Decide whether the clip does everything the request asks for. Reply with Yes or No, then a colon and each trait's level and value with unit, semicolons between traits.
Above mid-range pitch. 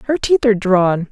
Yes: high, 215 Hz